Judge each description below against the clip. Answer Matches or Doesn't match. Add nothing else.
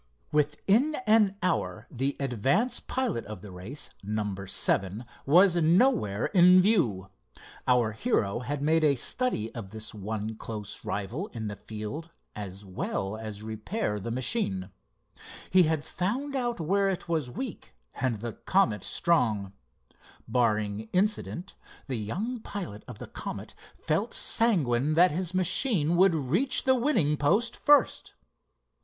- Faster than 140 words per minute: Doesn't match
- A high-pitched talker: Doesn't match